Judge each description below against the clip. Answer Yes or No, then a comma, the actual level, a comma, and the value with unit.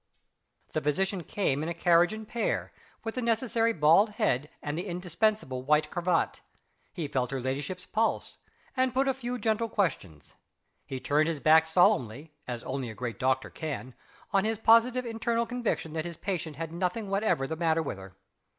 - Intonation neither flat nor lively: No, wide, 7.1 semitones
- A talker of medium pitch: Yes, medium, 170 Hz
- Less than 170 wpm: No, average, 180 wpm